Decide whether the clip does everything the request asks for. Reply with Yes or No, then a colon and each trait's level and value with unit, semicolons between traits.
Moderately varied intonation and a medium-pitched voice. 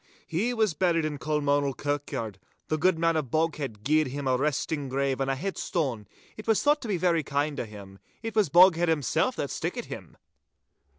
Yes: average, 4.1 semitones; medium, 150 Hz